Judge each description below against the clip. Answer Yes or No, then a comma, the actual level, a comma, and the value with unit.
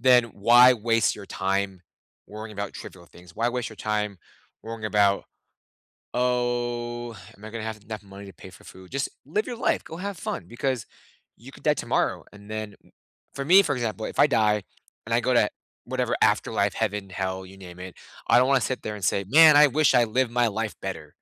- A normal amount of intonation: Yes, average, 3.5 semitones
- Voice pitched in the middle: No, low, 110 Hz